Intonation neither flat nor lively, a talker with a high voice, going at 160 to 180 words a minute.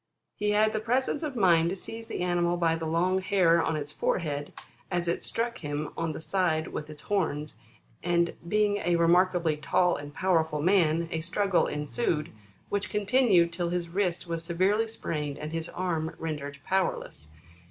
No: average, 3.2 semitones; medium, 170 Hz; average, 175 wpm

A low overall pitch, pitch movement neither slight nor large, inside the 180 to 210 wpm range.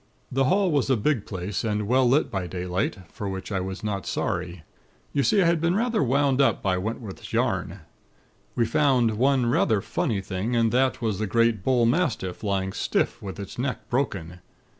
No: low, 115 Hz; wide, 5.7 semitones; average, 185 wpm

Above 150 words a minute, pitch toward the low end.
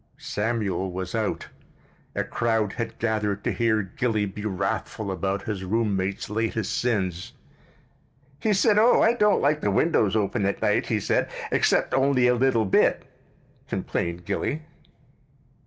No: average, 140 wpm; low, 110 Hz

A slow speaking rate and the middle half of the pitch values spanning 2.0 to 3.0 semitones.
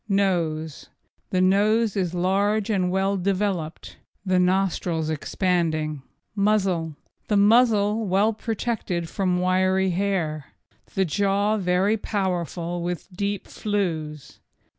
Yes: slow, 105 wpm; average, 2.7 semitones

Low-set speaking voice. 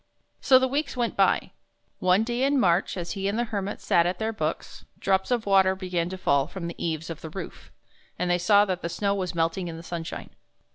No: high, 190 Hz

